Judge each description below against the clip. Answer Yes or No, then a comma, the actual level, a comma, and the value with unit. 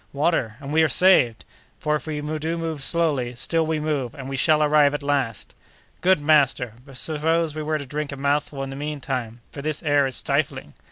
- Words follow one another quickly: Yes, fast, 215 wpm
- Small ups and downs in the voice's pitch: Yes, narrow, 2.3 semitones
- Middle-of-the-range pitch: Yes, medium, 150 Hz